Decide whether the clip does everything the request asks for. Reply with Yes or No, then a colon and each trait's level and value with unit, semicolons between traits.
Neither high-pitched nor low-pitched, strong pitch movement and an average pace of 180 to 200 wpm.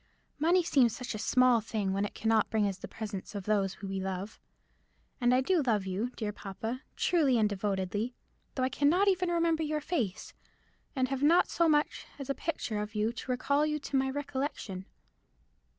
No: high, 245 Hz; wide, 5.8 semitones; average, 190 wpm